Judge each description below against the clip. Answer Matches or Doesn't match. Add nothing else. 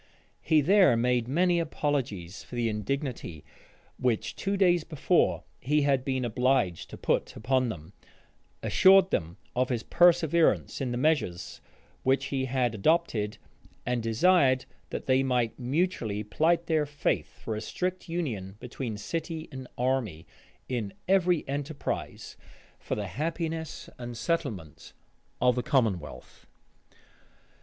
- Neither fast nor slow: Doesn't match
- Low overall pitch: Matches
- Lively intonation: Matches